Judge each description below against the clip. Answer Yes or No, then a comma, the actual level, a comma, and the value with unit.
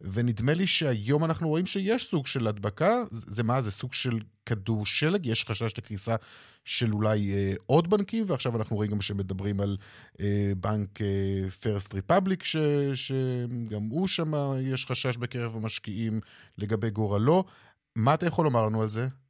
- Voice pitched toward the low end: Yes, low, 115 Hz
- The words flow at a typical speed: No, fast, 160 wpm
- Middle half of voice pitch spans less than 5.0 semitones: No, wide, 5.4 semitones